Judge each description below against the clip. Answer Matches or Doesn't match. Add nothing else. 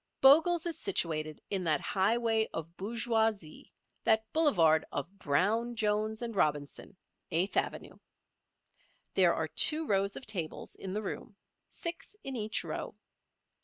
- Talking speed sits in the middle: Doesn't match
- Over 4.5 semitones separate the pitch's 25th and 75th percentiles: Matches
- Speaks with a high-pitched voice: Matches